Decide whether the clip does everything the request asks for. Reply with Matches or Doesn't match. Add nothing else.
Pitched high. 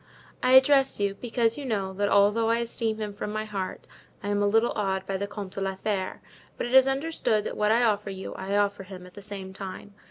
Matches